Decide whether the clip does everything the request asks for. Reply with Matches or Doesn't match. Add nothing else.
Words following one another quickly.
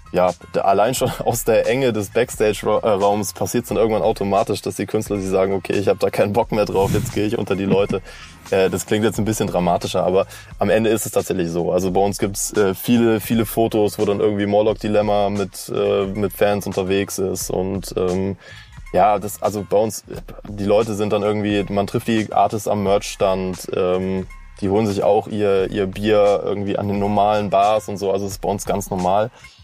Matches